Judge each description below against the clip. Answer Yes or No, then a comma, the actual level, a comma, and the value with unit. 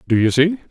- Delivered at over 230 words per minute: Yes, fast, 255 wpm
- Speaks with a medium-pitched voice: Yes, medium, 150 Hz